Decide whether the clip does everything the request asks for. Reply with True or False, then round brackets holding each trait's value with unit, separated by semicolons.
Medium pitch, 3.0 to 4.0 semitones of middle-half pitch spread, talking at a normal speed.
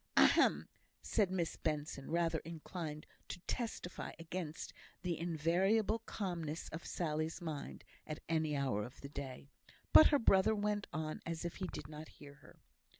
True (165 Hz; 3.3 semitones; 150 wpm)